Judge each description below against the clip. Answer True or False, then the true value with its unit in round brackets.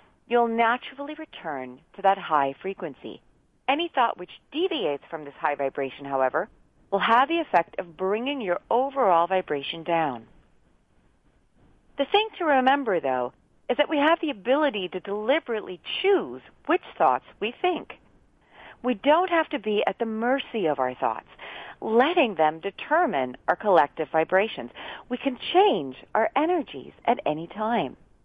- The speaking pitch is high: True (220 Hz)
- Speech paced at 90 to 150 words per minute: True (145 wpm)